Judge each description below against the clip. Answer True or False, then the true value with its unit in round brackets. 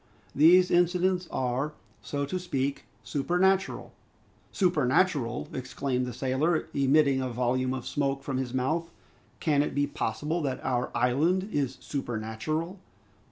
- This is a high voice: False (140 Hz)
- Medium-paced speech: False (130 wpm)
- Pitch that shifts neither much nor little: True (4.7 semitones)